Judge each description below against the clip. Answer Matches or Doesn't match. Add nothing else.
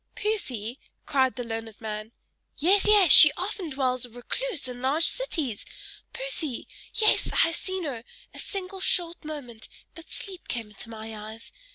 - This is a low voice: Doesn't match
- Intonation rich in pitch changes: Matches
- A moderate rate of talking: Matches